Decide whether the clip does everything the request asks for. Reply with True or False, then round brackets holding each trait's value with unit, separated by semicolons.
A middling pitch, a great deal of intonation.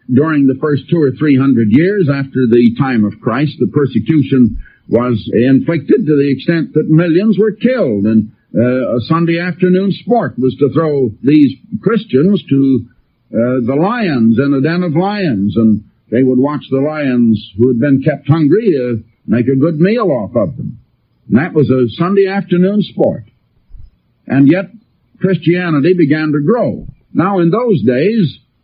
True (145 Hz; 5.8 semitones)